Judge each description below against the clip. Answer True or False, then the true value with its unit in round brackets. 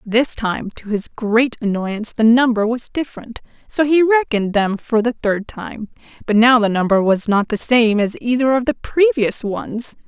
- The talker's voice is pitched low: False (225 Hz)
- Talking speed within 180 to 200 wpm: True (190 wpm)